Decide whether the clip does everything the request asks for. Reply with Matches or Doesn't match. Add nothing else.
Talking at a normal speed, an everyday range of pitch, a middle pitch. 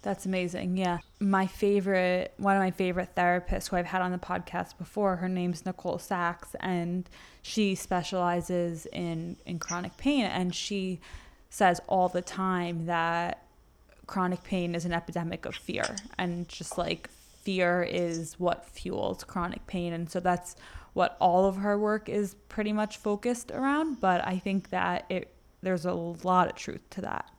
Doesn't match